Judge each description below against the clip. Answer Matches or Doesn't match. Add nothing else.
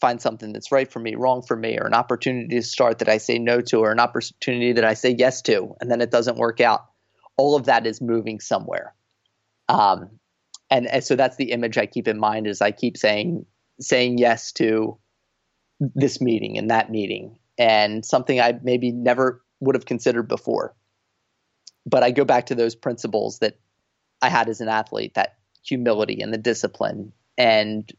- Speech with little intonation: Matches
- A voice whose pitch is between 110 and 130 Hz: Matches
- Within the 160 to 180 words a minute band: Doesn't match